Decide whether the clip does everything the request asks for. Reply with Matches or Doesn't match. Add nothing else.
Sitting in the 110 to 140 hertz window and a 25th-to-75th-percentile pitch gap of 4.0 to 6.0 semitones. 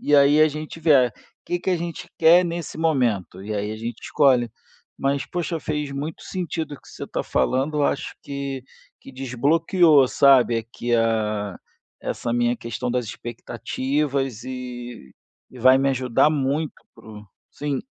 Matches